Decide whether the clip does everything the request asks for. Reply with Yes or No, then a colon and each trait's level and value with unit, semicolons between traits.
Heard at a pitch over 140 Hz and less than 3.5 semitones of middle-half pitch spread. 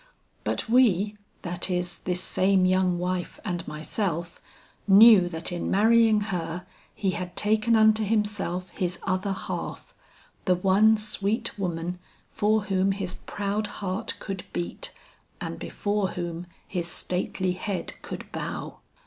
Yes: high, 190 Hz; average, 2.8 semitones